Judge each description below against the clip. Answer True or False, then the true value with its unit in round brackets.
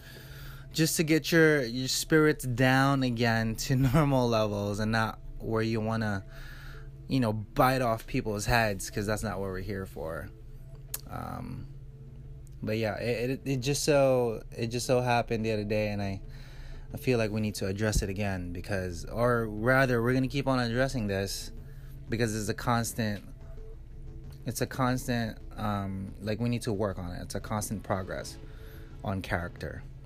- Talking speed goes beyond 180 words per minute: False (175 wpm)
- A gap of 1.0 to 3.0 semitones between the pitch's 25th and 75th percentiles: False (3.8 semitones)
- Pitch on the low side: True (120 Hz)